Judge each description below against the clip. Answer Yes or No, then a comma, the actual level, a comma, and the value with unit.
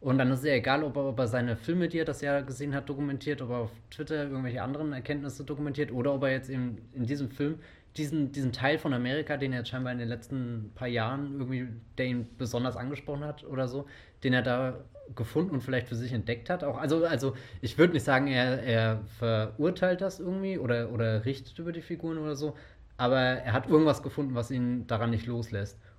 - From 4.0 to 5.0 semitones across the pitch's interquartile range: No, average, 3.2 semitones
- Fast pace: Yes, fast, 220 wpm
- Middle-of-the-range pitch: No, low, 130 Hz